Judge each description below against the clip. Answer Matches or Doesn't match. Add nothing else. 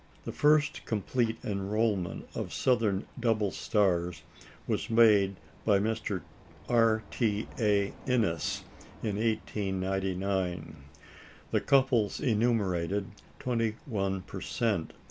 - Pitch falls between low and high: Doesn't match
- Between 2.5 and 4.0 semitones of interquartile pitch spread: Matches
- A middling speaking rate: Doesn't match